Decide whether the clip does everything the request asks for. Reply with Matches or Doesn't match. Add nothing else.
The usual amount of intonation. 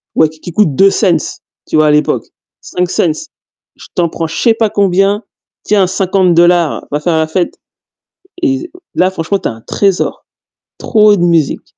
Matches